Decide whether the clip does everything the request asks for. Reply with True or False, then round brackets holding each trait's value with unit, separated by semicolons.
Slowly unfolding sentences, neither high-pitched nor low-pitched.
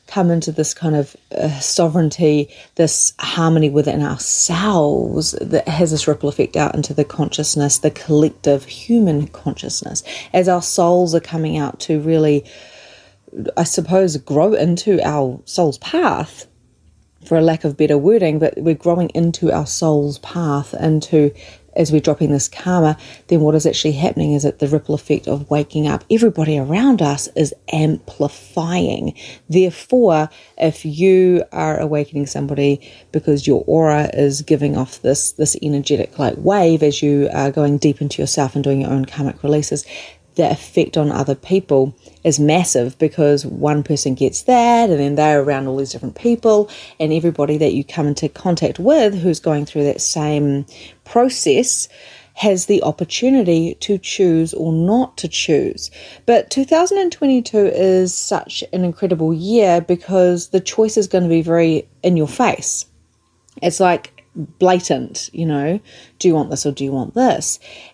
False (160 wpm; 155 Hz)